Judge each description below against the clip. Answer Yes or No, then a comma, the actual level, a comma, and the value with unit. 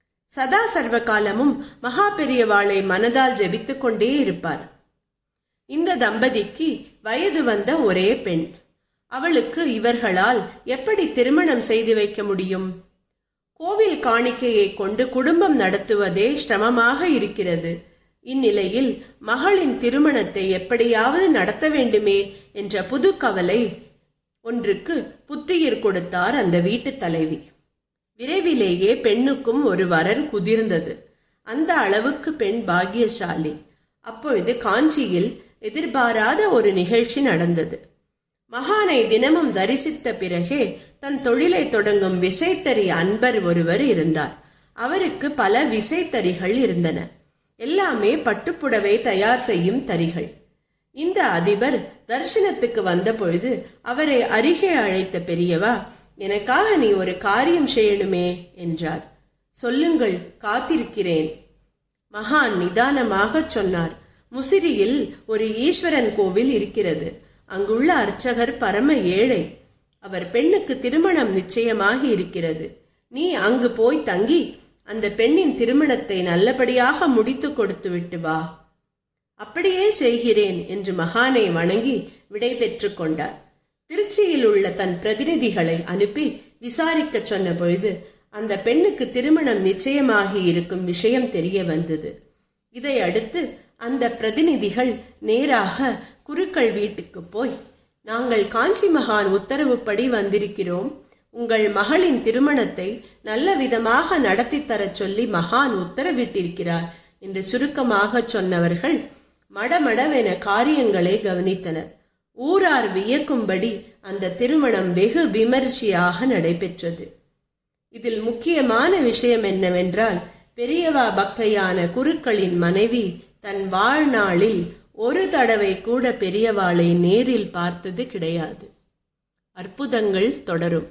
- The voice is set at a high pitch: Yes, high, 230 Hz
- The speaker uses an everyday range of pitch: No, wide, 6.2 semitones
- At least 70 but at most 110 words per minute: Yes, average, 90 wpm